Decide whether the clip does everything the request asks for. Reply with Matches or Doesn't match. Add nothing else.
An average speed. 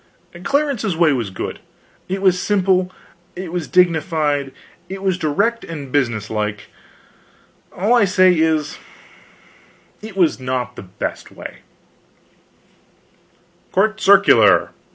Doesn't match